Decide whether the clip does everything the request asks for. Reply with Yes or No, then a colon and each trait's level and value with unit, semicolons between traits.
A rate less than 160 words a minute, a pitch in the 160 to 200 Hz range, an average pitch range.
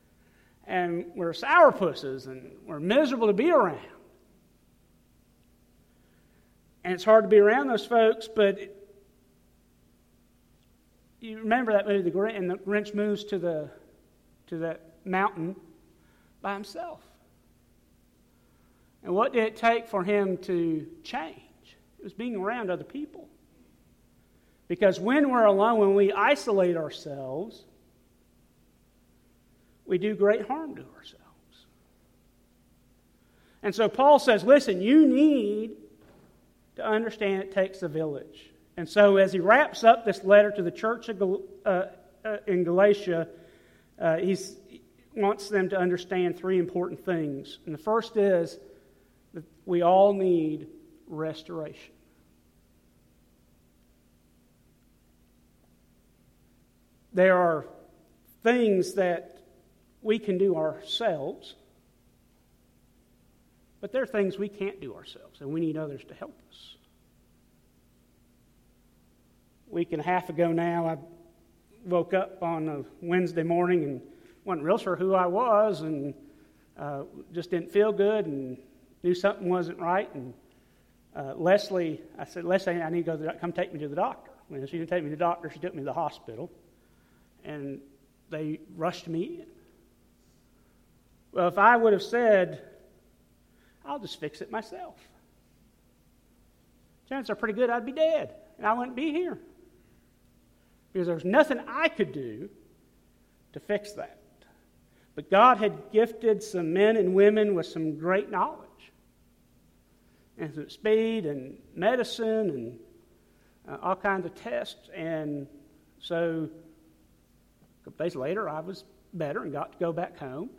Yes: slow, 135 wpm; high, 190 Hz; average, 4.5 semitones